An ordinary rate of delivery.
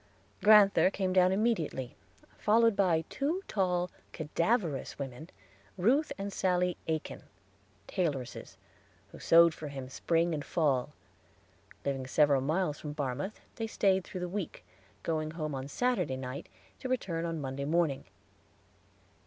No: slow, 130 wpm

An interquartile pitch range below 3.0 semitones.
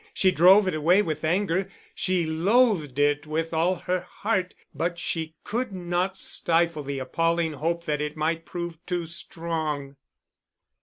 Yes: narrow, 2.6 semitones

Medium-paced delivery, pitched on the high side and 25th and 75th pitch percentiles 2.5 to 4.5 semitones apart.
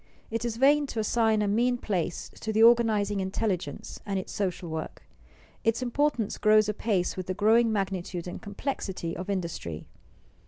Yes: average, 160 wpm; high, 210 Hz; average, 3.5 semitones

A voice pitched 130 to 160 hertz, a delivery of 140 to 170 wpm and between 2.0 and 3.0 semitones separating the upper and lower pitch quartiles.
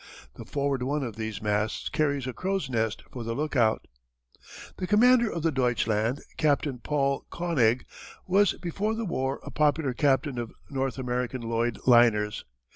No: low, 135 Hz; average, 155 wpm; average, 4.7 semitones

